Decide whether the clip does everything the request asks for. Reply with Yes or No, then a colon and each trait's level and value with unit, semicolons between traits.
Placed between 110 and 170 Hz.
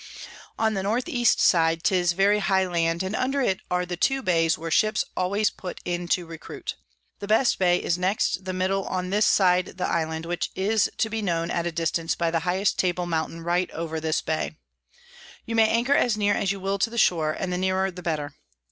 No: medium, 180 Hz